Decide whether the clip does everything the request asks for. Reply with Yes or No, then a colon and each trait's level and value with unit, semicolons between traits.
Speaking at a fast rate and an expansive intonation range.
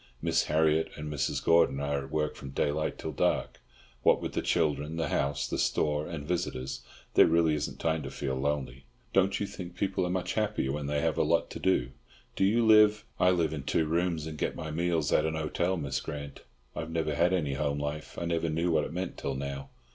No: fast, 225 wpm; average, 2.9 semitones